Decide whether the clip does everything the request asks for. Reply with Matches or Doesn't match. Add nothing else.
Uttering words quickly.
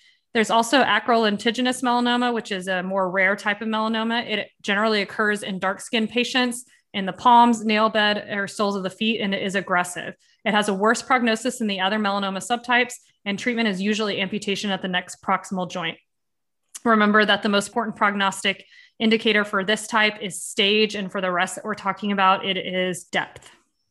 Doesn't match